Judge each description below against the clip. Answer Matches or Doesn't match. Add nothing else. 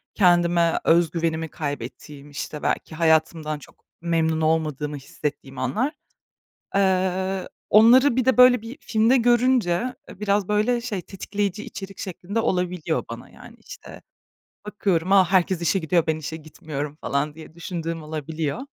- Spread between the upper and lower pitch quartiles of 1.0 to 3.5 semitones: Doesn't match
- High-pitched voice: Doesn't match